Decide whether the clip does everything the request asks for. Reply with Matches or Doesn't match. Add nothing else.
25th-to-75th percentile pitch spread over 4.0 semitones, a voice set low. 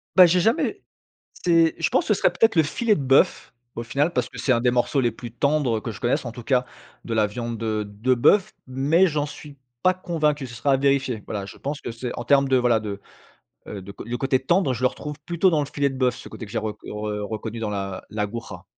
Matches